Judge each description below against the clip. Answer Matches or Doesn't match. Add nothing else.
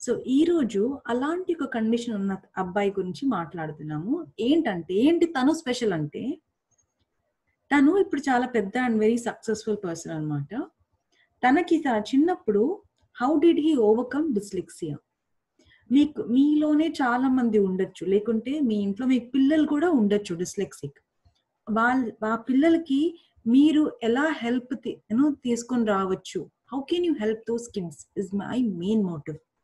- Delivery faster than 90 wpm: Matches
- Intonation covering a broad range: Matches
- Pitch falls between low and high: Doesn't match